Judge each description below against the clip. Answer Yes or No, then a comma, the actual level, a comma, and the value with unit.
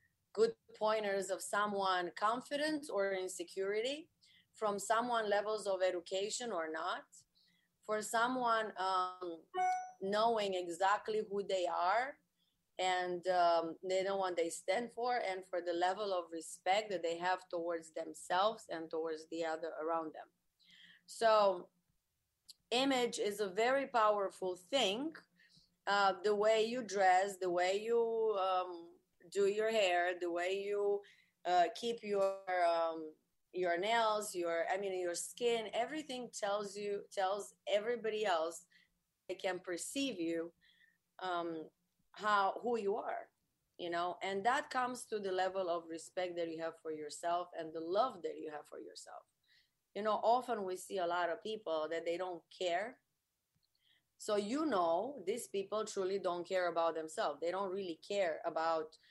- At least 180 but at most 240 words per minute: No, average, 150 wpm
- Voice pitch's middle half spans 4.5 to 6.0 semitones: No, average, 3.8 semitones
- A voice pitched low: No, high, 190 Hz